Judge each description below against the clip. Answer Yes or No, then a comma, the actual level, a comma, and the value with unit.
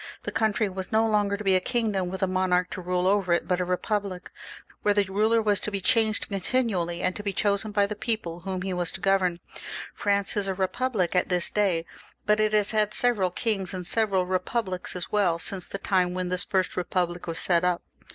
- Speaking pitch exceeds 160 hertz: Yes, high, 190 Hz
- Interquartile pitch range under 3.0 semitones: Yes, narrow, 2.6 semitones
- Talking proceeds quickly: Yes, fast, 220 wpm